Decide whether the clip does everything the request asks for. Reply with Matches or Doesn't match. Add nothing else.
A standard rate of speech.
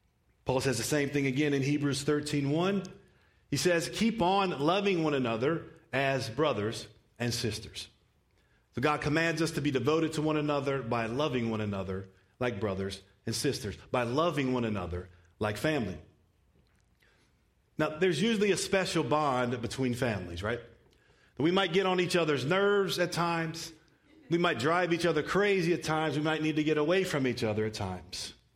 Matches